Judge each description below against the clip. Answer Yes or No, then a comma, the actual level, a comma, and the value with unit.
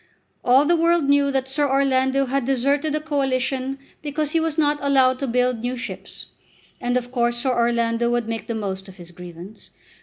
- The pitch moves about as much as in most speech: Yes, average, 3.0 semitones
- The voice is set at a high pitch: Yes, very high, 260 Hz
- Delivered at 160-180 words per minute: No, average, 190 wpm